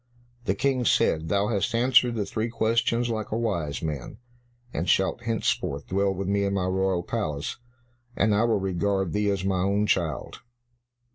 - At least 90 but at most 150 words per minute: No, average, 170 wpm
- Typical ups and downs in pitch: Yes, average, 3.3 semitones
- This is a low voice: Yes, low, 100 Hz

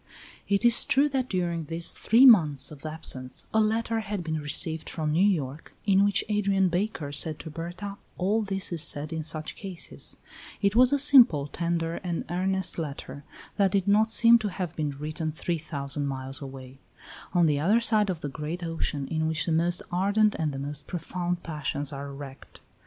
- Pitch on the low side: No, medium, 170 Hz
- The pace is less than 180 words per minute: No, average, 190 wpm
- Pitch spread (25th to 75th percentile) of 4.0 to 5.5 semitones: Yes, average, 5.0 semitones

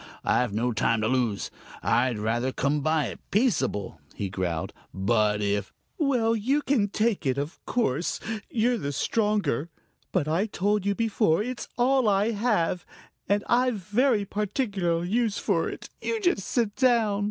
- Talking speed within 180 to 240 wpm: No, average, 160 wpm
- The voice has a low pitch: No, high, 200 Hz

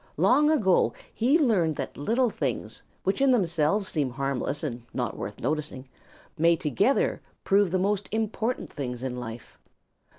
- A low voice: No, medium, 175 Hz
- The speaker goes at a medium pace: Yes, average, 145 wpm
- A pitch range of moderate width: No, wide, 7.5 semitones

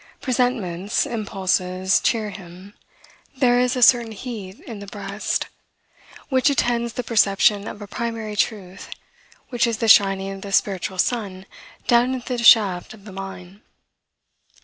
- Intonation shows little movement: No, average, 3.6 semitones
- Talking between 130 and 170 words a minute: Yes, average, 145 wpm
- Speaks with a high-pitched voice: Yes, high, 210 Hz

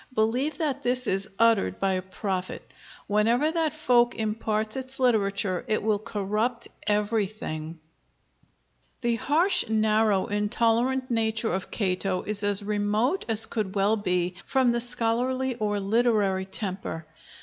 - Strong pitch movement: No, average, 3.2 semitones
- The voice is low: No, high, 215 Hz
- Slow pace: Yes, slow, 130 wpm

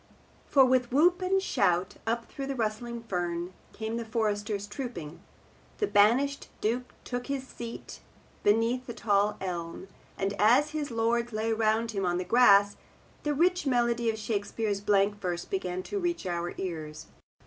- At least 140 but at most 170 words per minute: Yes, average, 160 wpm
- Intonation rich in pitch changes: No, average, 3.9 semitones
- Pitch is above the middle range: Yes, high, 225 Hz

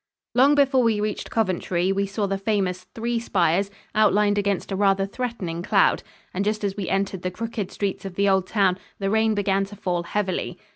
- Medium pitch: No, high, 200 Hz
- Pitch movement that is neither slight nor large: No, narrow, 2.1 semitones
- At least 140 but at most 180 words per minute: No, average, 195 wpm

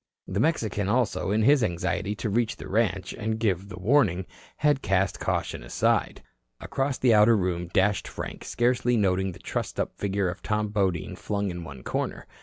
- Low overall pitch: Yes, low, 100 Hz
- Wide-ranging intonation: No, average, 3.8 semitones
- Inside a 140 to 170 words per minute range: No, average, 180 wpm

